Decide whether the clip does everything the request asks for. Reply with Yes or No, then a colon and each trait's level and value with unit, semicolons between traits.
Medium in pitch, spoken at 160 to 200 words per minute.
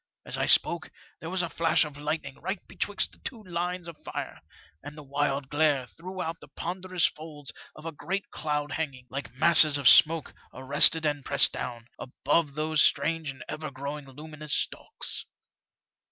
Yes: medium, 155 Hz; average, 175 wpm